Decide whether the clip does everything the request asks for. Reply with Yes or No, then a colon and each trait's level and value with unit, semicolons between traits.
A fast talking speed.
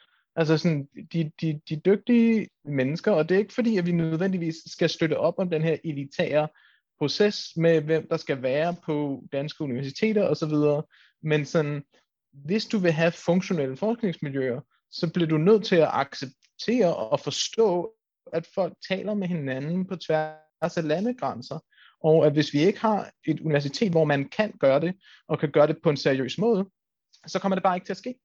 No: average, 185 wpm